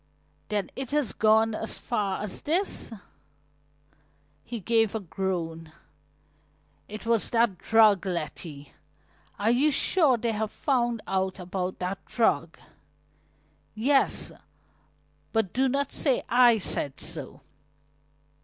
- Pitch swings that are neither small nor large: Yes, average, 4.1 semitones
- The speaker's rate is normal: No, slow, 115 wpm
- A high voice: Yes, high, 220 Hz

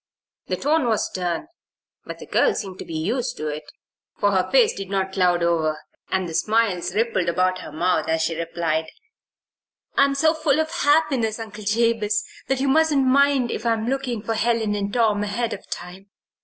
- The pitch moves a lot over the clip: Yes, wide, 5.9 semitones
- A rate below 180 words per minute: No, average, 185 wpm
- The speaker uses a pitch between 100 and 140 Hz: No, high, 215 Hz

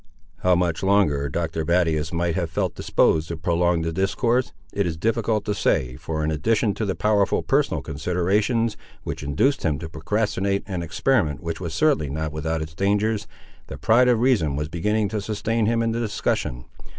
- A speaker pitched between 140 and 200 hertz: No, very low, 90 Hz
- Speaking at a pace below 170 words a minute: No, average, 185 wpm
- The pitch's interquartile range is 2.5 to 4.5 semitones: No, average, 5.1 semitones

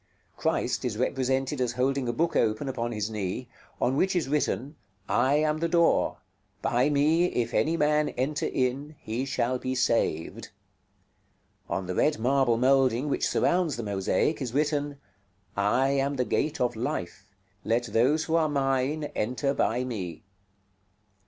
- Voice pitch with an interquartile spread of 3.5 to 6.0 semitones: Yes, average, 3.8 semitones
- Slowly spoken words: No, average, 155 wpm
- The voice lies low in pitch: Yes, low, 130 Hz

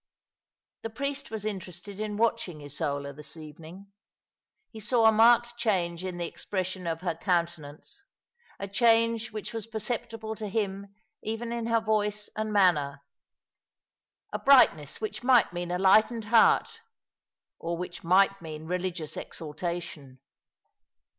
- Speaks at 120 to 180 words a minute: Yes, average, 140 wpm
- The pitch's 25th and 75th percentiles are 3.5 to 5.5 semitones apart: Yes, average, 4.7 semitones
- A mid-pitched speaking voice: No, high, 195 Hz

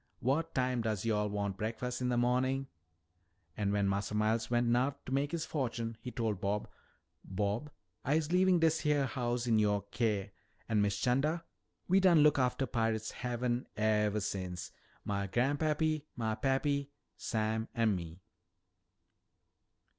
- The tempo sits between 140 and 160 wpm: Yes, average, 145 wpm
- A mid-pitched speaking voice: No, low, 120 Hz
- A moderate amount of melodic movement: Yes, average, 4.4 semitones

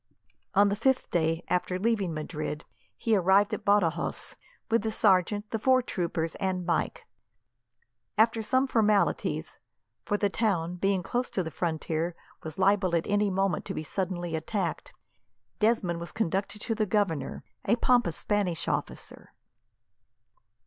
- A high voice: Yes, high, 195 Hz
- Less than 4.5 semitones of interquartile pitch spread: Yes, average, 3.7 semitones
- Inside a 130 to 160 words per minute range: Yes, average, 140 wpm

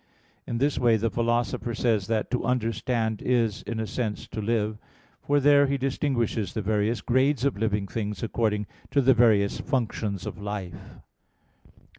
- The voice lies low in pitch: Yes, low, 115 Hz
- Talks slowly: No, average, 160 wpm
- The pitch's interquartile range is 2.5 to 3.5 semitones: Yes, average, 3.1 semitones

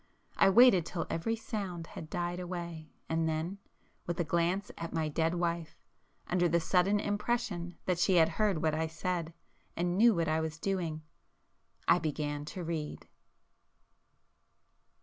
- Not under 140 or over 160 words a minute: Yes, average, 150 wpm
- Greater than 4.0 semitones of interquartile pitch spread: No, narrow, 2.4 semitones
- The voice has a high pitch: No, medium, 170 Hz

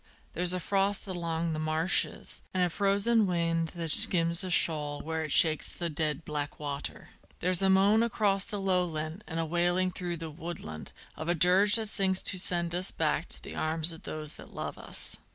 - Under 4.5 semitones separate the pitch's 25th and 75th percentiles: Yes, average, 2.9 semitones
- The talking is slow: No, average, 195 wpm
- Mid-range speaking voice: Yes, medium, 170 Hz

